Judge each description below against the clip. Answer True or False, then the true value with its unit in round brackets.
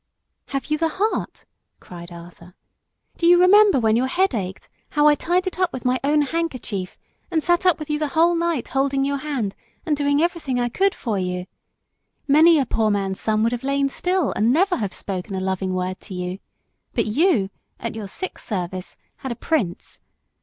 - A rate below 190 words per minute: False (195 wpm)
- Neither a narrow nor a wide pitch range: False (8.7 semitones)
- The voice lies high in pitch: True (270 Hz)